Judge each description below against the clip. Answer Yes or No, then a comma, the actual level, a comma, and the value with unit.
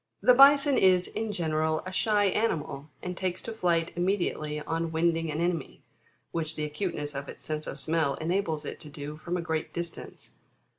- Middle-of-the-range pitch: Yes, medium, 165 Hz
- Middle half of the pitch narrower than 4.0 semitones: Yes, average, 3.2 semitones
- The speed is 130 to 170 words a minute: No, average, 190 wpm